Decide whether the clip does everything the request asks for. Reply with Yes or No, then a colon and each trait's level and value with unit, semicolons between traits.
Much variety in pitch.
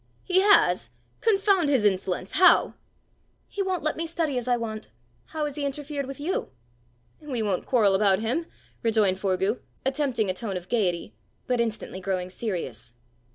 Yes: wide, 7.6 semitones